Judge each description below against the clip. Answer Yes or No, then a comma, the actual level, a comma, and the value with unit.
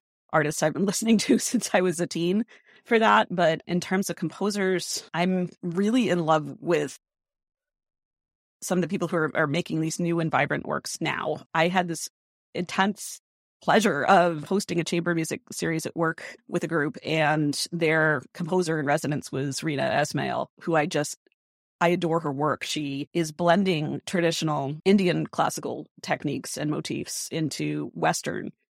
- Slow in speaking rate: No, average, 165 wpm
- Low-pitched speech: No, medium, 170 Hz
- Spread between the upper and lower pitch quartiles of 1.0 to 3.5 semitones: Yes, average, 2.8 semitones